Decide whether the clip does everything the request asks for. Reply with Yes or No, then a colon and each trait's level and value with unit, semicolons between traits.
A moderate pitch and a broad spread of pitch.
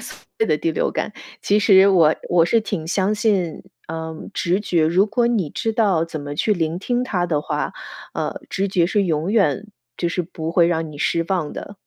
No: medium, 180 Hz; average, 4.2 semitones